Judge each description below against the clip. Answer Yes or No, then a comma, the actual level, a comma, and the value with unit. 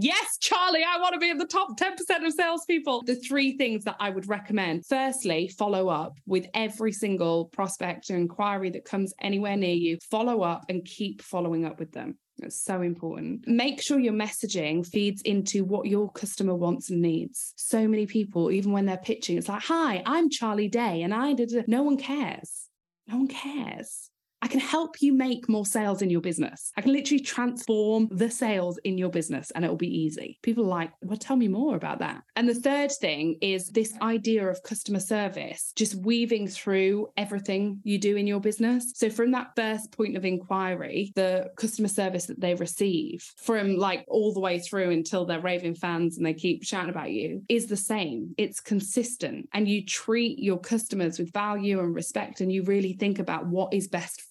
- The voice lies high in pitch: Yes, high, 205 Hz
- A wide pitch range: No, average, 4.2 semitones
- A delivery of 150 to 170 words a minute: No, average, 200 wpm